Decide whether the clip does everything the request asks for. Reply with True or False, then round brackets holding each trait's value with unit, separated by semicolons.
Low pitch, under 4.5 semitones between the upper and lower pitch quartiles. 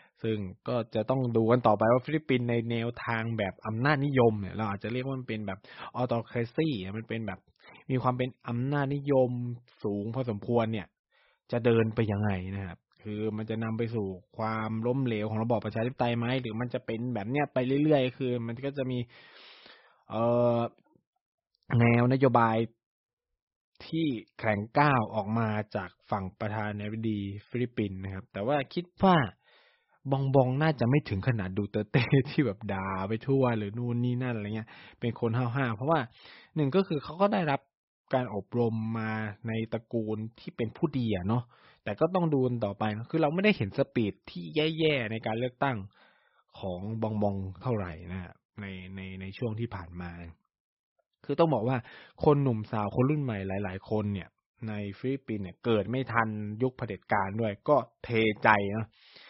True (115 Hz; 3.4 semitones)